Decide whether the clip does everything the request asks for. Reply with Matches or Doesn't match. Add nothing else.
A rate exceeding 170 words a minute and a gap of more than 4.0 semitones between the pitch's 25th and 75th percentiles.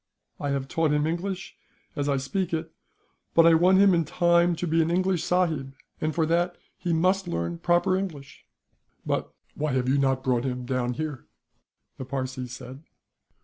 Matches